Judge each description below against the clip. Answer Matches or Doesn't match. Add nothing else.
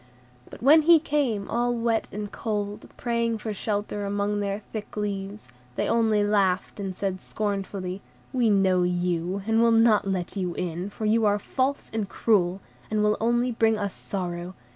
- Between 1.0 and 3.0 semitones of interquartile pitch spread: Matches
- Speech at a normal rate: Matches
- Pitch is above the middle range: Matches